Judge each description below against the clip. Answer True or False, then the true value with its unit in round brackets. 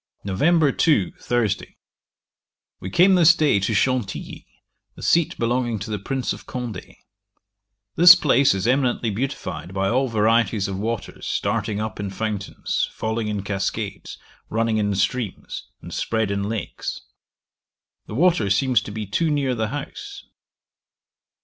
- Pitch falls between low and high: False (115 Hz)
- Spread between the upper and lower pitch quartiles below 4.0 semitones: False (4.7 semitones)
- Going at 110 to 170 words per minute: True (140 wpm)